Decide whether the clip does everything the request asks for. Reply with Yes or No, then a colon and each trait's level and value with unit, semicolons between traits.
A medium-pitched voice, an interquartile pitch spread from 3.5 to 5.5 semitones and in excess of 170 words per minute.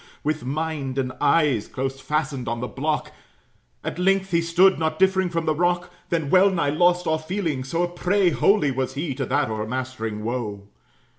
Yes: medium, 155 Hz; average, 5.1 semitones; average, 180 wpm